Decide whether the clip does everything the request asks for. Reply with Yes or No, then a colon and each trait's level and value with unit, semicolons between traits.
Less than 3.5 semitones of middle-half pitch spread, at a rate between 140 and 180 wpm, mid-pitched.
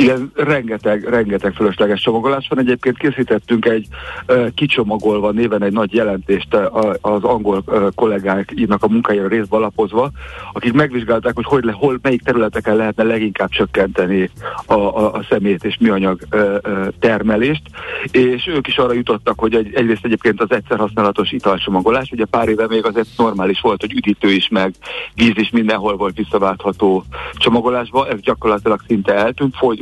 No: average, 2.7 semitones; average, 150 wpm; low, 110 Hz